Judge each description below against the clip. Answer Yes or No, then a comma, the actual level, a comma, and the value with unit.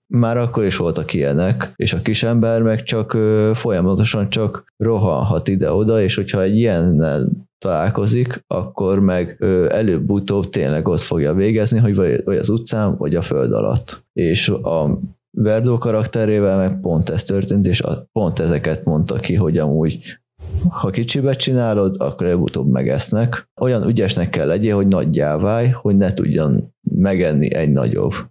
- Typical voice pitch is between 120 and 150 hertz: No, low, 105 Hz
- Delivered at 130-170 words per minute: Yes, average, 150 wpm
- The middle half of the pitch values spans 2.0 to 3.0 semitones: No, average, 3.4 semitones